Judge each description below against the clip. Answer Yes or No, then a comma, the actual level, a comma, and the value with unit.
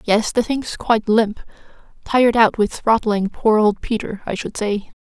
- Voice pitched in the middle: No, high, 220 Hz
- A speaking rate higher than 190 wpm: No, average, 180 wpm